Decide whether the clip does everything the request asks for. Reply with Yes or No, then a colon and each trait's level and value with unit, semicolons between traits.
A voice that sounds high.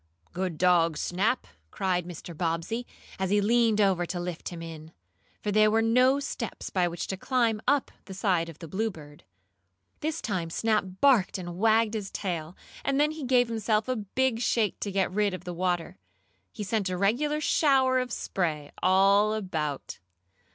Yes: high, 200 Hz